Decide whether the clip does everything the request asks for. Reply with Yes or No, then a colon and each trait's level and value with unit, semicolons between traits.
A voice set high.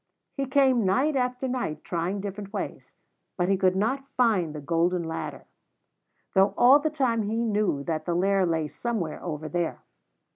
Yes: high, 200 Hz